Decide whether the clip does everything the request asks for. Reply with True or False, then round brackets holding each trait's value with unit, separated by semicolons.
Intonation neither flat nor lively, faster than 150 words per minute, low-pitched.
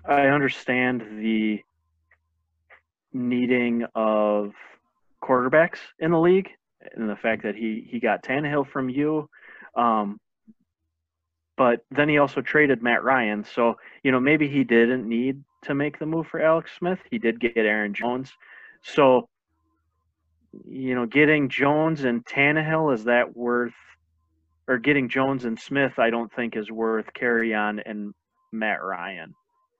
False (5.0 semitones; 145 wpm; 120 Hz)